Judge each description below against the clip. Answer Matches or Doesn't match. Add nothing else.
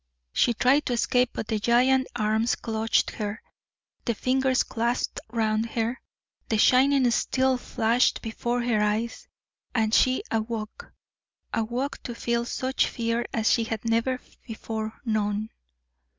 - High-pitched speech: Matches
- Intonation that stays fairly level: Matches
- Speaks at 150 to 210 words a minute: Doesn't match